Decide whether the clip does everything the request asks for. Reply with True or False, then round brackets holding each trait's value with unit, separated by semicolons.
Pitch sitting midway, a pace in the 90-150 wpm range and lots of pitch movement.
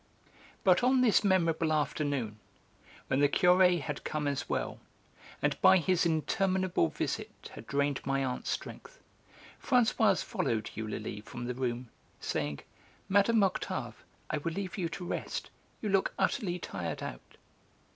True (165 Hz; 140 wpm; 6.3 semitones)